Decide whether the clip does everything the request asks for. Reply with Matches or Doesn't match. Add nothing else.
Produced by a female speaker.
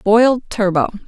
Matches